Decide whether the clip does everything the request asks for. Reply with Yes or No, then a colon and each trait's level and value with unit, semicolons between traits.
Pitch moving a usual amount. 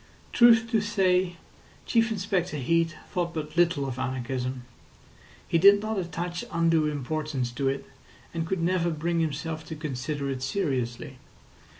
Yes: average, 4.6 semitones